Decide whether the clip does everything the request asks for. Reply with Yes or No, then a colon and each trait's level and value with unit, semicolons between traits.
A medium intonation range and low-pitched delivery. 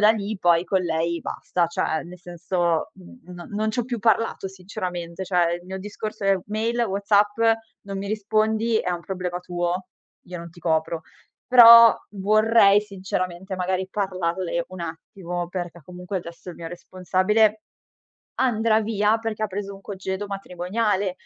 No: average, 3.1 semitones; high, 190 Hz